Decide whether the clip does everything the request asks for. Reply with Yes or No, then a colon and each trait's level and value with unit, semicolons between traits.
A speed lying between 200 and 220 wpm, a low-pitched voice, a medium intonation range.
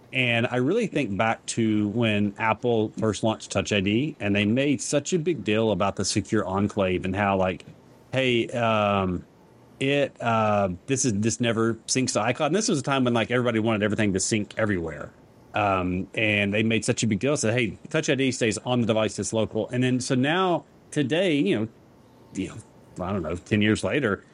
Yes: fast, 205 wpm; low, 110 Hz; average, 3.3 semitones